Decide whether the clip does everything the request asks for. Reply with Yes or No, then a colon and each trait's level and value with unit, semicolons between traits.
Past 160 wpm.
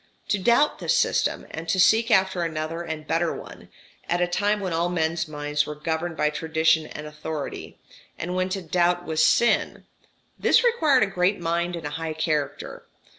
Yes: average, 180 wpm